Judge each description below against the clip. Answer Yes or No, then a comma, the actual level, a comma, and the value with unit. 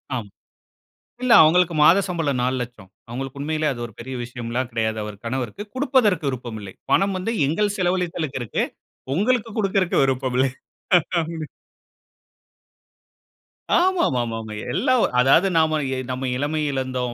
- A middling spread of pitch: No, wide, 6.4 semitones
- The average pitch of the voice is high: No, medium, 145 Hz